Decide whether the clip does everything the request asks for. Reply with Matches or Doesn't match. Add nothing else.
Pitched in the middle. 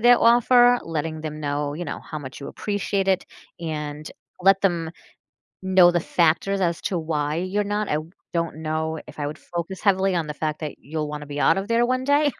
Matches